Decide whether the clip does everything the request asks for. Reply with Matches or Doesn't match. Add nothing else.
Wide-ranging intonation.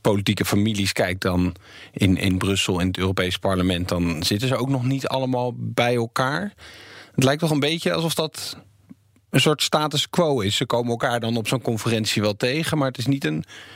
Matches